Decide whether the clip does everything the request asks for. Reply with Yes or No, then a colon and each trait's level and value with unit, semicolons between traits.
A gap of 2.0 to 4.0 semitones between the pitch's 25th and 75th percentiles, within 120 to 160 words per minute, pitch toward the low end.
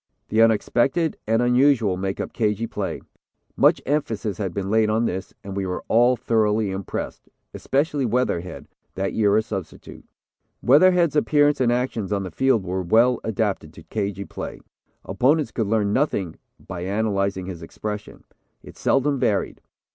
No: average, 4.4 semitones; average, 155 wpm; low, 110 Hz